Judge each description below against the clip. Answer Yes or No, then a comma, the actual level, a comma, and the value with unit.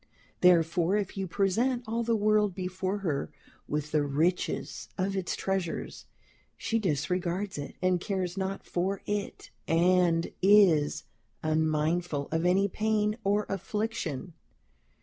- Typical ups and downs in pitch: Yes, average, 3.5 semitones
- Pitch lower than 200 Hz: Yes, medium, 185 Hz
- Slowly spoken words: Yes, slow, 125 wpm